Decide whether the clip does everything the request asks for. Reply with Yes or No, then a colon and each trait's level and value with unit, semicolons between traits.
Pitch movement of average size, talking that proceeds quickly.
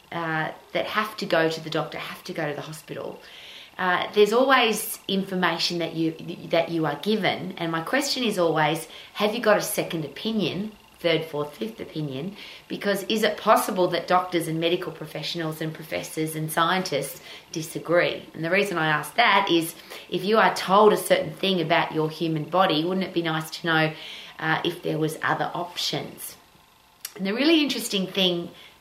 No: average, 3.7 semitones; average, 185 wpm